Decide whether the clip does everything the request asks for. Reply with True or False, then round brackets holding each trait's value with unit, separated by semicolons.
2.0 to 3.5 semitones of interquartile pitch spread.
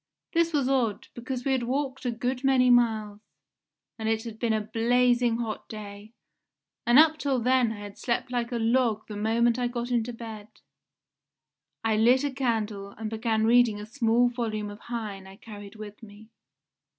True (2.4 semitones)